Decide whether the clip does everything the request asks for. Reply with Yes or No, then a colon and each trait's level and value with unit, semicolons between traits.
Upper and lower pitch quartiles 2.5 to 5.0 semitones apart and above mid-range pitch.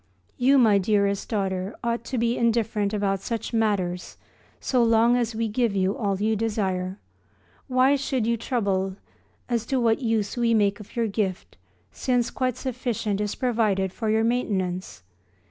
Yes: average, 3.1 semitones; high, 220 Hz